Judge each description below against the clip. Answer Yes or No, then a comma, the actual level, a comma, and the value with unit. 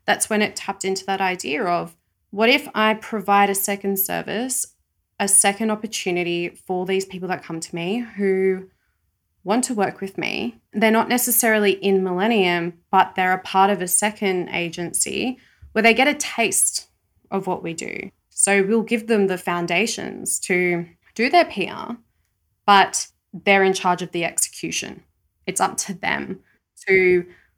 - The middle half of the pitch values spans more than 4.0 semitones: No, average, 3.1 semitones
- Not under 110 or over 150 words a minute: No, average, 165 wpm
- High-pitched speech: Yes, high, 195 Hz